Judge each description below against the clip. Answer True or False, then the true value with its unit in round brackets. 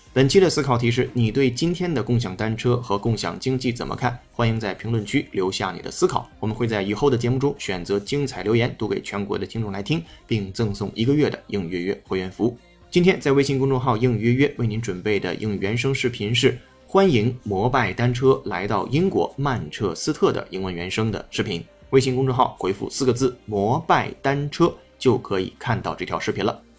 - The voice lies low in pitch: True (120 Hz)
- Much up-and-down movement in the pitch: False (4.0 semitones)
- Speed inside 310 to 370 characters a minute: True (325 characters per minute)